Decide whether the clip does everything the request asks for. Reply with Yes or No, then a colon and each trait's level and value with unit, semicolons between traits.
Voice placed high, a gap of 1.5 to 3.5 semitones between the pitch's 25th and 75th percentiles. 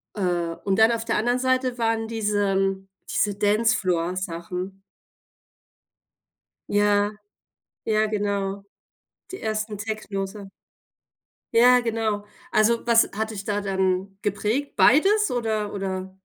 Yes: high, 205 Hz; narrow, 2.6 semitones